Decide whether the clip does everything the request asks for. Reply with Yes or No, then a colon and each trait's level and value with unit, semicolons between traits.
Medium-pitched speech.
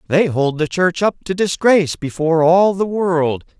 Yes: medium, 170 Hz